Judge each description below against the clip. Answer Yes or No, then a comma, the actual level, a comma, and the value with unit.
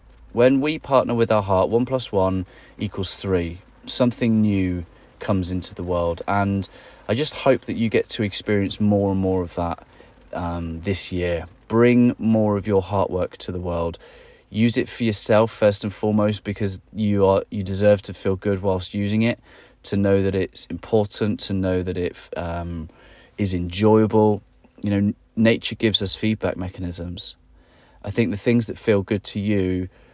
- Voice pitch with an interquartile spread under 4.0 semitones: Yes, average, 3.0 semitones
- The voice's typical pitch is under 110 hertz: Yes, low, 100 Hz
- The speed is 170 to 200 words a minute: Yes, average, 175 wpm